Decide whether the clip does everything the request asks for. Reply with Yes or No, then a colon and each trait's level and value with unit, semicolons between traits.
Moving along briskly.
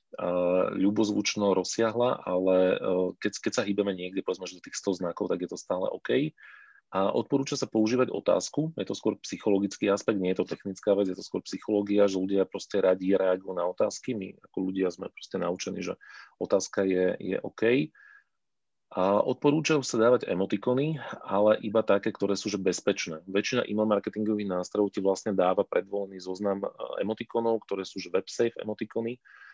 Yes: fast, 170 wpm